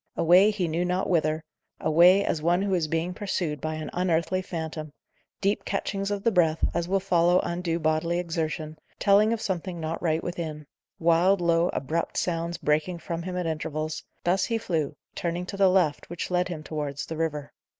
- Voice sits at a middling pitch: Yes, medium, 170 Hz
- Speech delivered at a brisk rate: No, average, 185 wpm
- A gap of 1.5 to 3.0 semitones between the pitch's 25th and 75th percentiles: Yes, narrow, 2.6 semitones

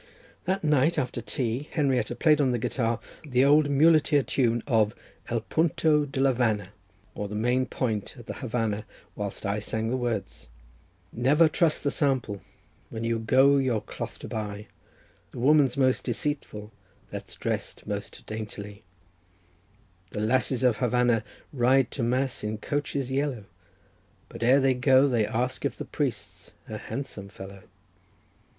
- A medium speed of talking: Yes, average, 150 wpm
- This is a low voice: Yes, low, 125 Hz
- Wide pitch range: No, average, 3.9 semitones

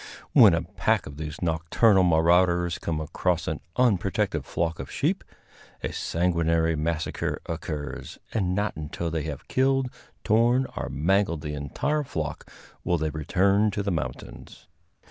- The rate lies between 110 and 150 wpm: Yes, average, 145 wpm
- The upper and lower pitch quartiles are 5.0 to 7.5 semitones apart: No, average, 4.1 semitones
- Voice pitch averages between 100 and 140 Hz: No, very low, 85 Hz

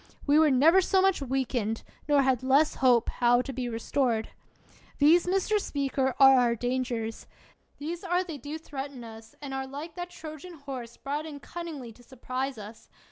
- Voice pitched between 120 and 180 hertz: No, very high, 270 Hz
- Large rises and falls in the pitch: No, average, 4.1 semitones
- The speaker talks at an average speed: Yes, average, 175 wpm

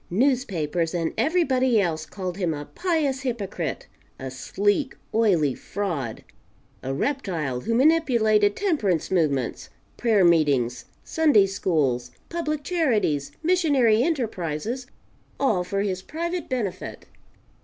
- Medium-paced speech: No, slow, 110 wpm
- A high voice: Yes, high, 205 Hz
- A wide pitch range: Yes, wide, 8.8 semitones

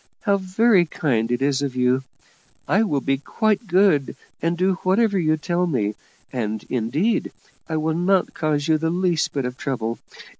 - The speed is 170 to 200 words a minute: Yes, average, 175 wpm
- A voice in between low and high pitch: Yes, medium, 155 Hz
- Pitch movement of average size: No, wide, 5.9 semitones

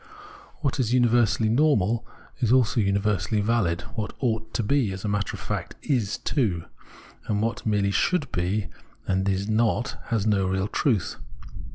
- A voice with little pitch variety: No, average, 3.1 semitones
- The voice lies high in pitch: No, low, 110 Hz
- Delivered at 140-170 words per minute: Yes, average, 165 wpm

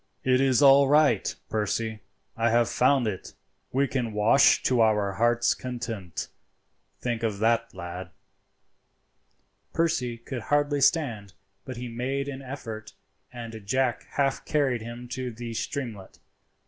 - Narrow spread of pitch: No, average, 3.2 semitones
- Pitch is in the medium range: No, low, 120 Hz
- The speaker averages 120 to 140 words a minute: Yes, slow, 135 wpm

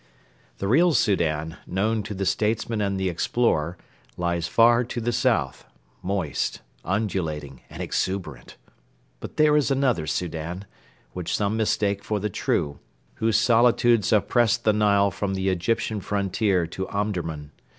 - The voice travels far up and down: No, average, 4.2 semitones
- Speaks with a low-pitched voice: Yes, low, 100 Hz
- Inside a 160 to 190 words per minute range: No, average, 140 wpm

